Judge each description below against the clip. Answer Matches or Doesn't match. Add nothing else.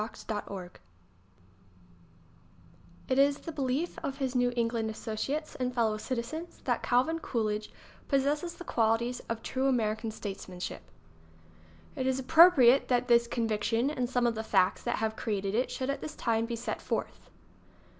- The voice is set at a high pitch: Matches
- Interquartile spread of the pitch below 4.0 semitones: Matches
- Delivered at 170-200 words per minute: Doesn't match